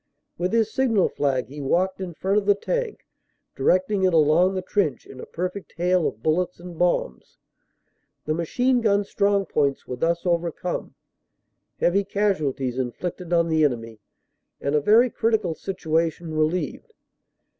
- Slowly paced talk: No, average, 150 wpm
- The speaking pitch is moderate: Yes, medium, 175 Hz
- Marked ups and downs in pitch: No, average, 4.4 semitones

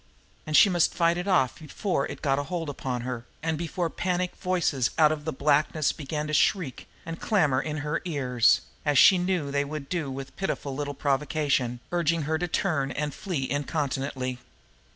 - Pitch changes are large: No, average, 3.6 semitones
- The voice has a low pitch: No, medium, 150 Hz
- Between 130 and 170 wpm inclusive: No, average, 185 wpm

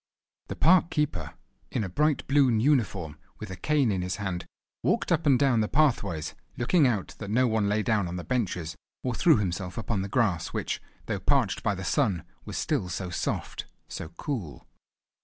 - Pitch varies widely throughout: Yes, wide, 6.8 semitones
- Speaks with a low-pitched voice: Yes, low, 110 Hz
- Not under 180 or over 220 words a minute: Yes, average, 190 wpm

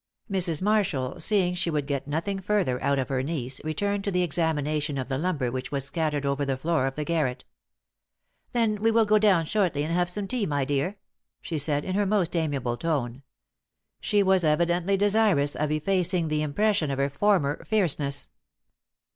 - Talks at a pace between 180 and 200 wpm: Yes, average, 185 wpm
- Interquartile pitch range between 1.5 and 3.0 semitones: No, wide, 5.5 semitones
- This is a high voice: No, medium, 160 Hz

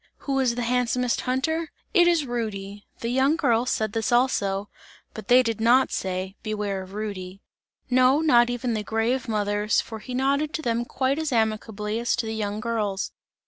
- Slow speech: No, average, 185 wpm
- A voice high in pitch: Yes, high, 235 Hz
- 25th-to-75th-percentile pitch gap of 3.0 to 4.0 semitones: Yes, average, 3.4 semitones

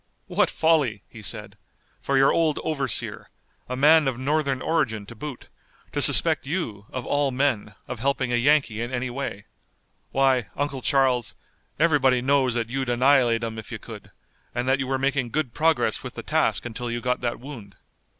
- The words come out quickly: No, average, 180 wpm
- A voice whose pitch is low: Yes, low, 130 Hz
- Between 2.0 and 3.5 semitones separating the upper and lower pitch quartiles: Yes, average, 2.9 semitones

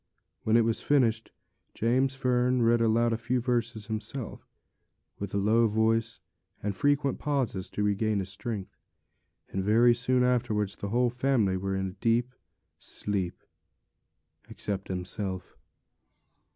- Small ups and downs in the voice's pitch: No, average, 3.3 semitones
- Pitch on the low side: Yes, low, 115 Hz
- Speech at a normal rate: No, slow, 130 wpm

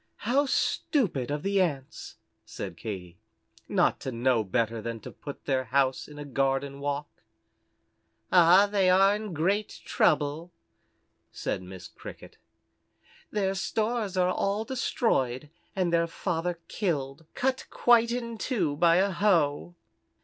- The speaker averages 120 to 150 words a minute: Yes, slow, 135 wpm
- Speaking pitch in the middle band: Yes, medium, 170 Hz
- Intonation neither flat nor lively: No, wide, 6.8 semitones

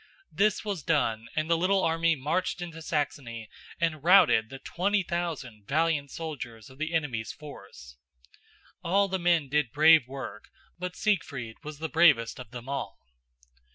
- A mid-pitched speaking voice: Yes, medium, 155 Hz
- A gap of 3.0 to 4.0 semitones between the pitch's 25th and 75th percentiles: No, average, 4.7 semitones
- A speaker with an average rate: Yes, average, 155 wpm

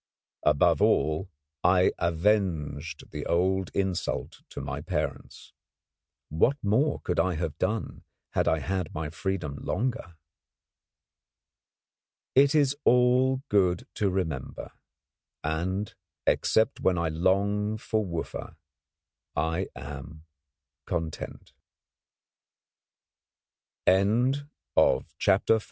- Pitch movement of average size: Yes, average, 4.8 semitones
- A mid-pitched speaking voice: No, very low, 95 Hz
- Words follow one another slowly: Yes, slow, 105 wpm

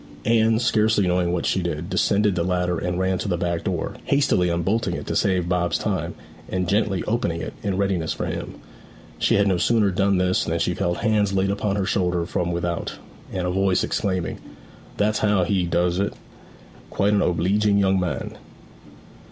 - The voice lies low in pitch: Yes, very low, 95 Hz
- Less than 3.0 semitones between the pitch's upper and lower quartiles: Yes, narrow, 2.5 semitones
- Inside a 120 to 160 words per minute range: No, average, 185 wpm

